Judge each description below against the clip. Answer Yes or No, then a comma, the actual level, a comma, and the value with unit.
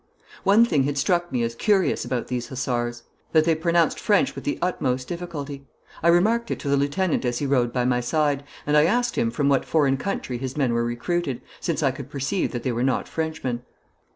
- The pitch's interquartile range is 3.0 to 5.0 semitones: No, wide, 5.5 semitones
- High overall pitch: No, medium, 140 Hz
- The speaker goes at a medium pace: No, fast, 215 wpm